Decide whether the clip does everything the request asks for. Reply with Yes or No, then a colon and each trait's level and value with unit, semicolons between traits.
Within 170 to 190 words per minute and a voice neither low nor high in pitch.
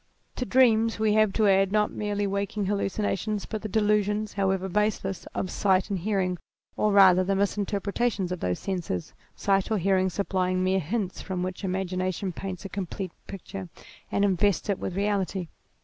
No: average, 180 wpm; high, 195 Hz